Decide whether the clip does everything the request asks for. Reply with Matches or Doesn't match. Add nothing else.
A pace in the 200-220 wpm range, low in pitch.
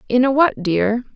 Doesn't match